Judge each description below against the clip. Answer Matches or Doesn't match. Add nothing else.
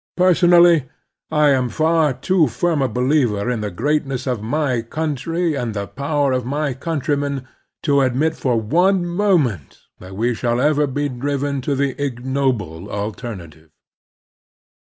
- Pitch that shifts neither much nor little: Matches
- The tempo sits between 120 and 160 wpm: Matches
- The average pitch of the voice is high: Doesn't match